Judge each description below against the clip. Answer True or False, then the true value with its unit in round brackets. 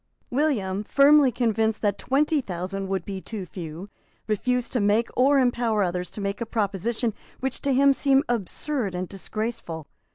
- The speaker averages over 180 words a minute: False (160 wpm)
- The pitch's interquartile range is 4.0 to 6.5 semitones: True (4.9 semitones)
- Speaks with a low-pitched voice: False (220 Hz)